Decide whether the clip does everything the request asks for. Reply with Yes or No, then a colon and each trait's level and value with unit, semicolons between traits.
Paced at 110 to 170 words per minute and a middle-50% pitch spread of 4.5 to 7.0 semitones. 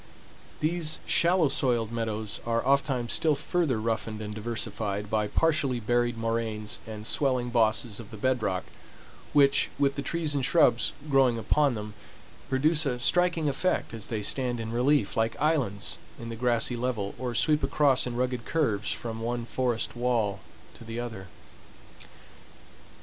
No: average, 155 wpm; average, 3.8 semitones